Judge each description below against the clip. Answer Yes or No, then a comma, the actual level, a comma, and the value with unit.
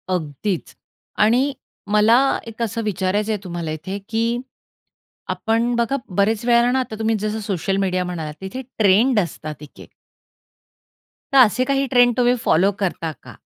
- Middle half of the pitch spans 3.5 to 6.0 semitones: Yes, average, 4.3 semitones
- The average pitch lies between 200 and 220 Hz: Yes, high, 215 Hz